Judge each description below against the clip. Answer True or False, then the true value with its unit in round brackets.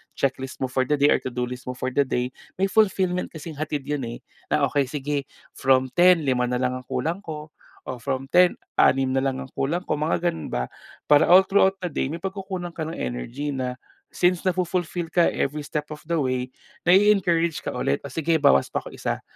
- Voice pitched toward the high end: False (150 Hz)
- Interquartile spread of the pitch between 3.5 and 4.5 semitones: False (5.1 semitones)